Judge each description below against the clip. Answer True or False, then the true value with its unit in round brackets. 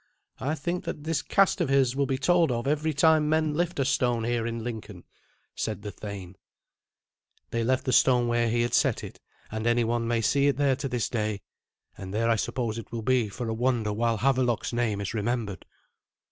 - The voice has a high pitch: False (120 Hz)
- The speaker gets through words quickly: True (210 wpm)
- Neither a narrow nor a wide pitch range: True (3.5 semitones)